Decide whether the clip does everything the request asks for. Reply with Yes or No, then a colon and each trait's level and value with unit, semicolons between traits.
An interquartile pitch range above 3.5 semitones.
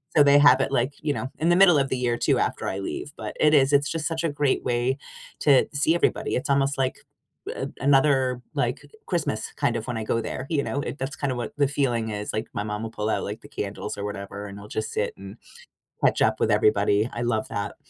Yes: average, 4.7 semitones